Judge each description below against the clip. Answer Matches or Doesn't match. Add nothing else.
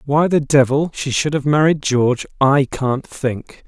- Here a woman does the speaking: Doesn't match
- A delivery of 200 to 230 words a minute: Doesn't match